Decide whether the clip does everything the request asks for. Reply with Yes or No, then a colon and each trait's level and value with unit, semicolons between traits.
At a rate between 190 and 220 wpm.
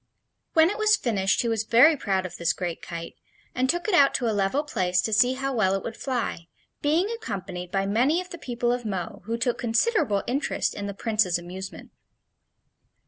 Yes: average, 200 wpm